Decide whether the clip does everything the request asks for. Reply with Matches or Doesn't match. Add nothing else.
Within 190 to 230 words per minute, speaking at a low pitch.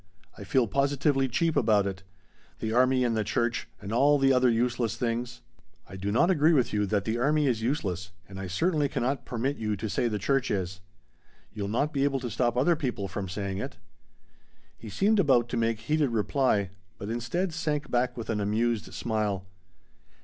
Matches